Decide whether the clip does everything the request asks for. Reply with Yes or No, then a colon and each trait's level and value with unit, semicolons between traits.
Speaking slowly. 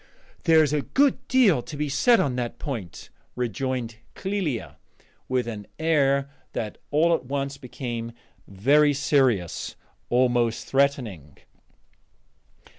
Yes: slow, 115 wpm